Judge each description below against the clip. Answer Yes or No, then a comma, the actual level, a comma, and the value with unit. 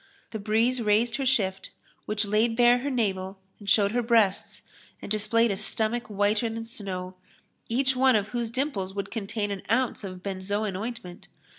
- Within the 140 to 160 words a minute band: No, average, 170 wpm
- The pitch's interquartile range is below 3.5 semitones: Yes, average, 2.9 semitones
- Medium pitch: No, high, 215 Hz